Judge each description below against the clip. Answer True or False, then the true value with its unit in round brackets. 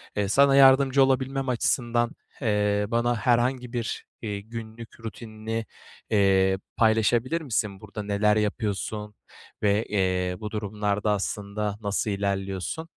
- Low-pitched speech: True (110 Hz)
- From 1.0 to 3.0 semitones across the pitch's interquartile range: True (2.7 semitones)